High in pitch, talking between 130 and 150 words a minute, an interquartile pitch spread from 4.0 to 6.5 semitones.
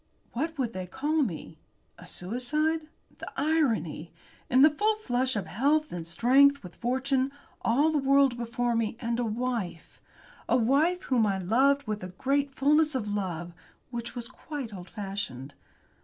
No: high, 245 Hz; average, 160 wpm; average, 5.3 semitones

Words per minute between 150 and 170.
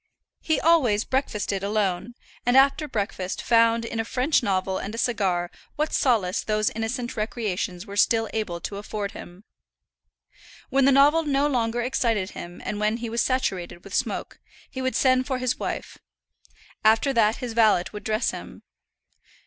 Yes: average, 165 wpm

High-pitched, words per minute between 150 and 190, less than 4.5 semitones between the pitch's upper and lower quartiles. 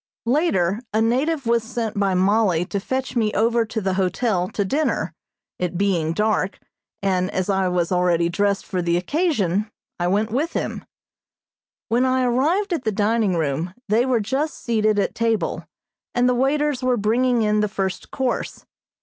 No: high, 215 Hz; average, 170 wpm; average, 4.8 semitones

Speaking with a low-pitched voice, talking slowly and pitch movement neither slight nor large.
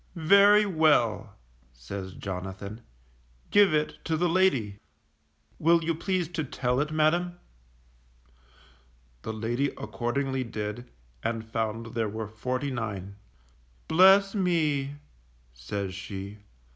No: low, 125 Hz; slow, 105 wpm; wide, 7.5 semitones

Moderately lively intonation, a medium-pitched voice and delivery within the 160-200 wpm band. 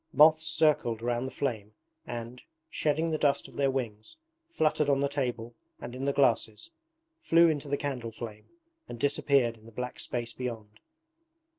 No: average, 3.8 semitones; low, 130 Hz; average, 165 wpm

